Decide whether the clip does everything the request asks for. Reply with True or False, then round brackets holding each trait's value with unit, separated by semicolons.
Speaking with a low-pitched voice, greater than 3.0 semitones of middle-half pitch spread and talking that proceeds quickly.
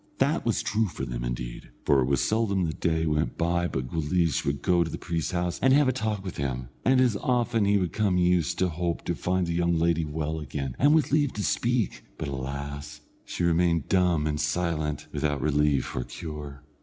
True (85 Hz; 4.2 semitones; 220 wpm)